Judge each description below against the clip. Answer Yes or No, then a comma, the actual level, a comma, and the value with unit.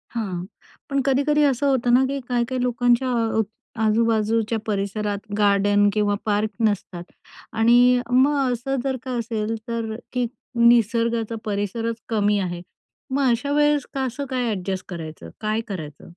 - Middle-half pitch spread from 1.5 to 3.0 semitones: No, average, 3.4 semitones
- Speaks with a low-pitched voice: No, high, 230 Hz